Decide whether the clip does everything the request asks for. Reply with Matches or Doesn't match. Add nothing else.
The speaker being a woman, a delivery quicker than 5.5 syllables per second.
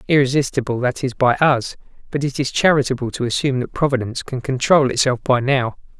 Doesn't match